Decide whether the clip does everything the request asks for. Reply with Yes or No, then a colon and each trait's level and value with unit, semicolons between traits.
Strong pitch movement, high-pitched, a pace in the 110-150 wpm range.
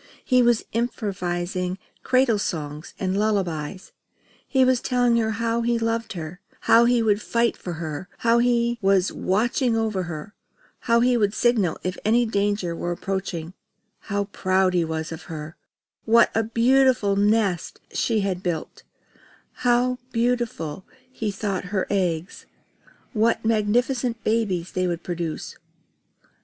No: average, 4.5 semitones; high, 205 Hz; average, 140 wpm